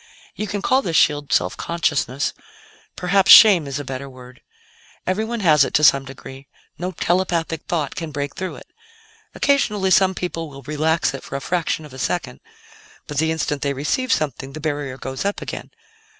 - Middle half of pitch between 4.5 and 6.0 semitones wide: Yes, average, 4.9 semitones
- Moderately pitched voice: Yes, medium, 155 Hz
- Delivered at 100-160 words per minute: No, average, 180 wpm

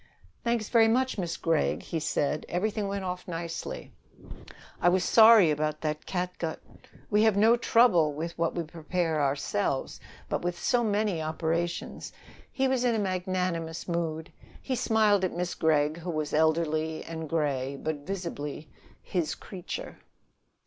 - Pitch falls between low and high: Yes, medium, 170 Hz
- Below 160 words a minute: Yes, average, 150 wpm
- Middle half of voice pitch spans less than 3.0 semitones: No, average, 4.2 semitones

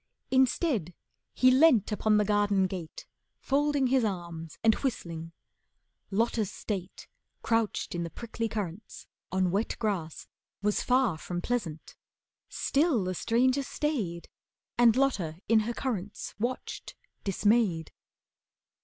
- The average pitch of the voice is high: Yes, high, 215 Hz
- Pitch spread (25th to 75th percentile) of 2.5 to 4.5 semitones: No, wide, 5.4 semitones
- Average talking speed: No, slow, 120 wpm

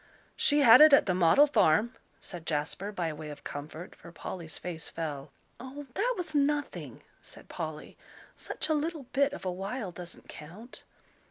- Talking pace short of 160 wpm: No, average, 170 wpm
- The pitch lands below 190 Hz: No, high, 195 Hz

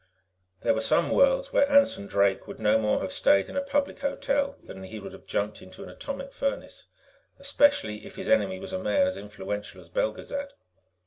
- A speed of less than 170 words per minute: No, average, 195 wpm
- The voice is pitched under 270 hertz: No, very high, 275 Hz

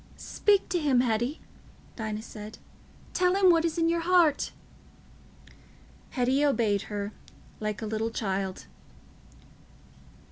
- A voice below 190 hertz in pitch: No, high, 245 Hz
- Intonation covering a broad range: Yes, wide, 7.5 semitones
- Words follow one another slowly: Yes, slow, 115 wpm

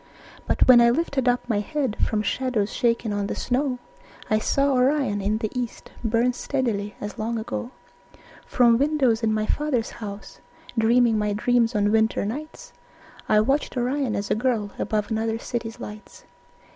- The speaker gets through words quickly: No, average, 165 wpm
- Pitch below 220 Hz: No, high, 230 Hz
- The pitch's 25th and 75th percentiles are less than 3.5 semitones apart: Yes, average, 3.0 semitones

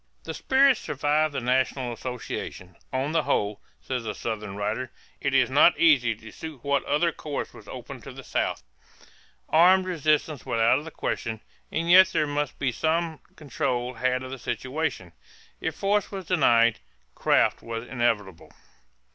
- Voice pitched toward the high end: No, low, 135 Hz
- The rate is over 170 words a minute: No, average, 165 wpm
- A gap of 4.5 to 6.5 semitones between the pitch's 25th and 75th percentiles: Yes, average, 5.1 semitones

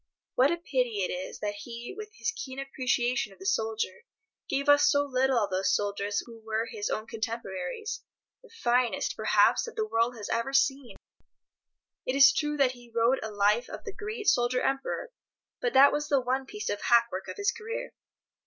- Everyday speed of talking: Yes, average, 190 wpm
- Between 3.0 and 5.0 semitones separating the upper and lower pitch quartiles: Yes, average, 4.3 semitones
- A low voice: No, very high, 250 Hz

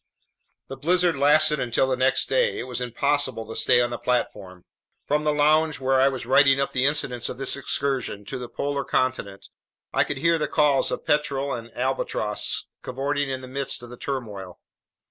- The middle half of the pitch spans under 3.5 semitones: Yes, average, 2.8 semitones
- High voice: No, low, 135 Hz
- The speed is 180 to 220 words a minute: Yes, average, 190 wpm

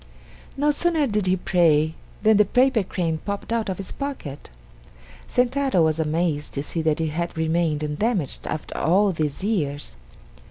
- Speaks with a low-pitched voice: No, medium, 175 Hz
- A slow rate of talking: No, average, 160 wpm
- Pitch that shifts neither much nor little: No, wide, 5.9 semitones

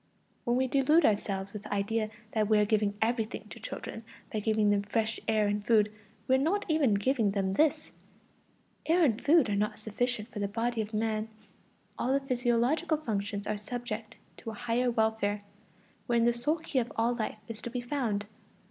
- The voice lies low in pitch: No, high, 225 Hz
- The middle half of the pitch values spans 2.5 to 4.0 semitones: Yes, average, 2.8 semitones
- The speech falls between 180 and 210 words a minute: Yes, average, 190 wpm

